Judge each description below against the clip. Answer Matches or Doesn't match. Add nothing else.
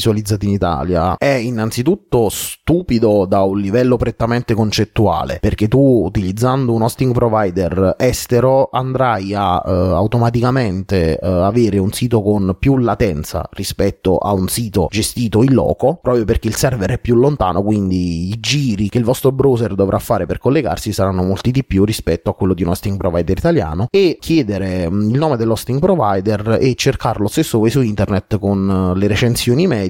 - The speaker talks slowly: Doesn't match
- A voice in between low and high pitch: Doesn't match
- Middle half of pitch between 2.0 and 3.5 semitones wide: Doesn't match